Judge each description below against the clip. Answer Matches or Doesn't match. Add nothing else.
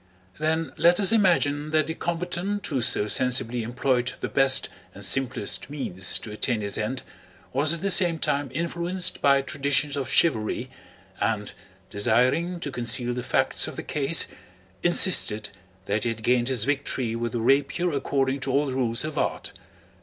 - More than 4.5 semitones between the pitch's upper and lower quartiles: Matches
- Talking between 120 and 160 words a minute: Doesn't match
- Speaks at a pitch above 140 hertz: Doesn't match